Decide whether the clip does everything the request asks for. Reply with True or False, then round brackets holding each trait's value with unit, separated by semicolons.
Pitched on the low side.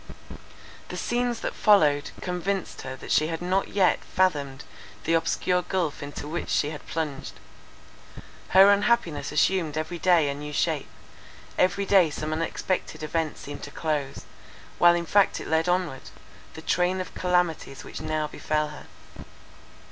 False (165 Hz)